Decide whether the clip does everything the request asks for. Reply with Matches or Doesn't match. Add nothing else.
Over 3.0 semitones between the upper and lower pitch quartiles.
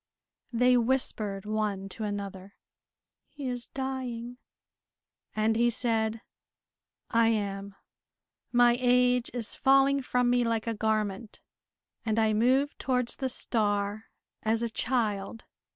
Doesn't match